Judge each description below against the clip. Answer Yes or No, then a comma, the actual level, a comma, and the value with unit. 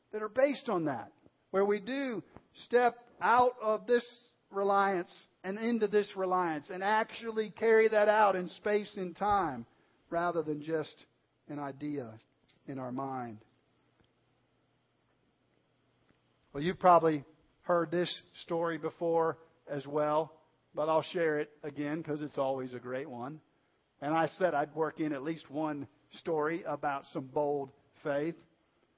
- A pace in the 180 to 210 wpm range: No, average, 140 wpm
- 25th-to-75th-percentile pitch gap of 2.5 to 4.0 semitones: No, average, 5.1 semitones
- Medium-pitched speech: Yes, medium, 160 Hz